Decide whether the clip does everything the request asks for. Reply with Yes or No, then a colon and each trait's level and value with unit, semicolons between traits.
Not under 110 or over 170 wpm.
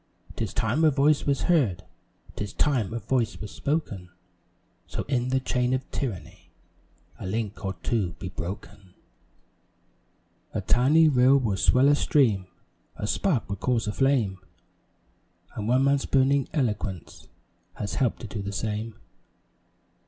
Yes: average, 145 wpm